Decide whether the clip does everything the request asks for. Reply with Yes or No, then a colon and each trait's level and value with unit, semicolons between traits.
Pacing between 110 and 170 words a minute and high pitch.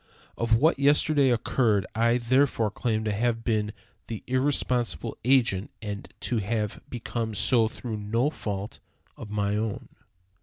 No: average, 140 wpm; low, 115 Hz